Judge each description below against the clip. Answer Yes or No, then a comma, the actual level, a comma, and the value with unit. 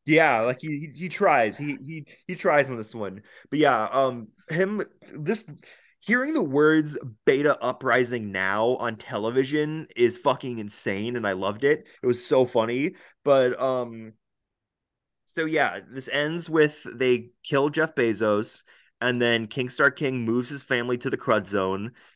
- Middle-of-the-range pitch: No, low, 130 Hz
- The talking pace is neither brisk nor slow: Yes, average, 155 wpm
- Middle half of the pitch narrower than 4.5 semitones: No, average, 4.9 semitones